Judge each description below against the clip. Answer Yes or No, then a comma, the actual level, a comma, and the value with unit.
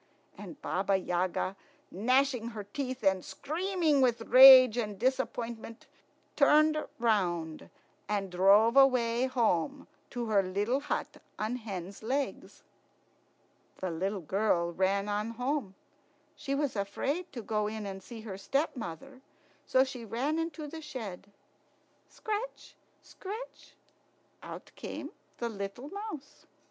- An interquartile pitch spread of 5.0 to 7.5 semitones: Yes, wide, 5.6 semitones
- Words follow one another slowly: Yes, slow, 120 wpm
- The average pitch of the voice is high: Yes, high, 230 Hz